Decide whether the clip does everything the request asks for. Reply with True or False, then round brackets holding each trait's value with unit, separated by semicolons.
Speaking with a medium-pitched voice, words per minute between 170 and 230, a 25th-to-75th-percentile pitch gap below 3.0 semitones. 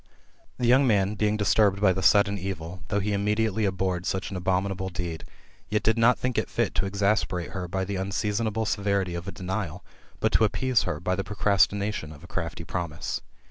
False (100 Hz; 200 wpm; 2.4 semitones)